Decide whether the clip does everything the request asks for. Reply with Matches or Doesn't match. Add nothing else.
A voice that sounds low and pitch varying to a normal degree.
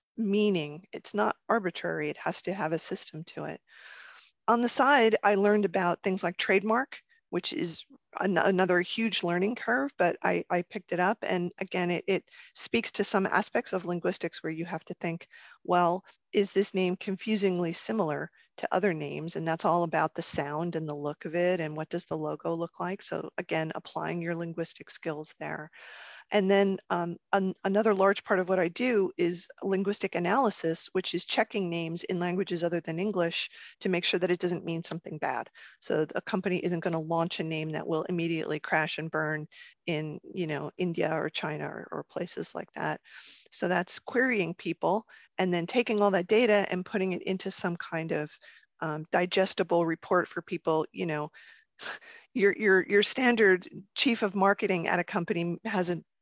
Doesn't match